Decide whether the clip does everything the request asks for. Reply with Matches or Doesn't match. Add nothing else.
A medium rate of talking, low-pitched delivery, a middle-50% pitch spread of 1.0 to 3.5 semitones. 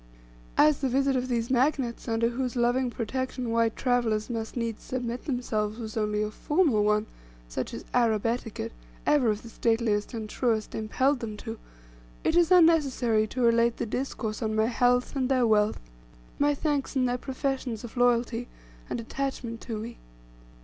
Doesn't match